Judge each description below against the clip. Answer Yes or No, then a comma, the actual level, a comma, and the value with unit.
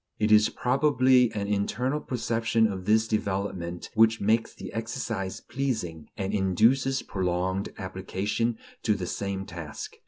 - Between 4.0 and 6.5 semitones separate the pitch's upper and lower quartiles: No, average, 3.5 semitones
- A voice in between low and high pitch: No, low, 105 Hz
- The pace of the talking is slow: Yes, slow, 130 wpm